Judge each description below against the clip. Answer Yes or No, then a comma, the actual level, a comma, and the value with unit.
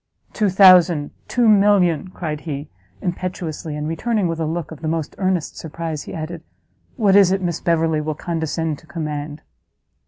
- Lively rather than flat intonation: No, average, 3.0 semitones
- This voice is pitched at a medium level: Yes, medium, 165 Hz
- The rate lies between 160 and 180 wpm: Yes, average, 165 wpm